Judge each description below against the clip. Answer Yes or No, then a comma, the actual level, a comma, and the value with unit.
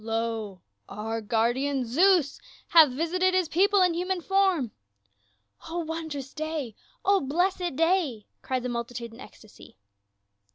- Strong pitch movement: Yes, wide, 7.5 semitones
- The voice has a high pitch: Yes, very high, 285 Hz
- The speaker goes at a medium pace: No, slow, 130 wpm